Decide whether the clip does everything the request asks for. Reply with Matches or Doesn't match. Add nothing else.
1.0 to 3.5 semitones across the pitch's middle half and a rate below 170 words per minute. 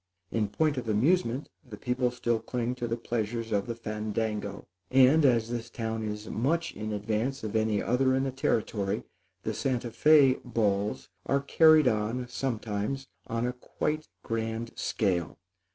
Matches